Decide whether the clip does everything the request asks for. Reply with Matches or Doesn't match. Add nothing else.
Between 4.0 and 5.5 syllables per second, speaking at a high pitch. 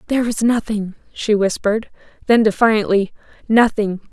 Matches